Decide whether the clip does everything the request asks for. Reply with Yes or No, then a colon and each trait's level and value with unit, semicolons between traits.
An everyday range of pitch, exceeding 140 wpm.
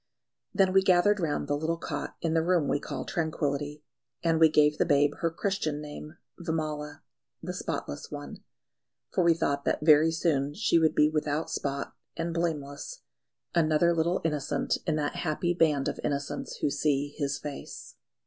No: narrow, 2.3 semitones; average, 170 wpm